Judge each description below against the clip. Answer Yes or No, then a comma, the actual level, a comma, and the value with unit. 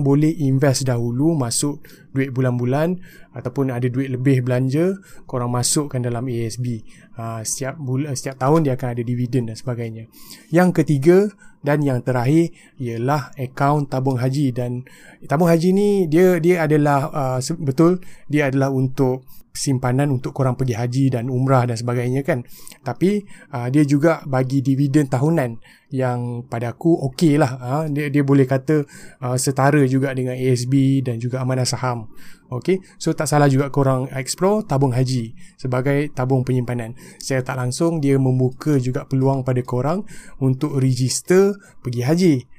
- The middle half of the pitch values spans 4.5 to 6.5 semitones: No, average, 3.4 semitones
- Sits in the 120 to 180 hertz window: Yes, low, 135 Hz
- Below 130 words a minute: No, average, 150 wpm